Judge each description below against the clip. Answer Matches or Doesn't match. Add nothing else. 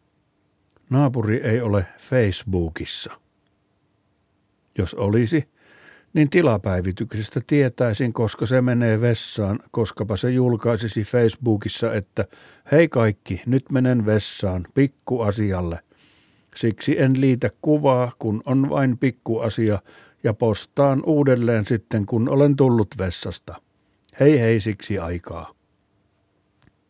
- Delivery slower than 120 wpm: Matches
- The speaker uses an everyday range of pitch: Matches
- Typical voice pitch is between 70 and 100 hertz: Doesn't match